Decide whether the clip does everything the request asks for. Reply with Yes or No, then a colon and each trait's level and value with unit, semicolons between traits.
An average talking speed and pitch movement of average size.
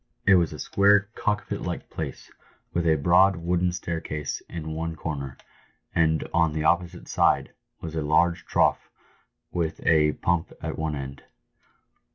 No: average, 150 wpm; narrow, 2.1 semitones